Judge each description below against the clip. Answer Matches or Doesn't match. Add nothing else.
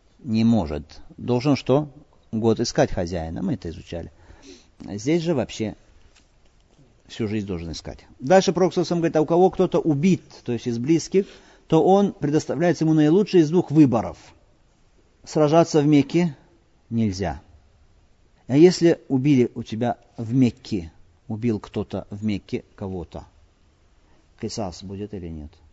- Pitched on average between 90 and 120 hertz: Matches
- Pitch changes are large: Matches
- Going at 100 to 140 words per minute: Matches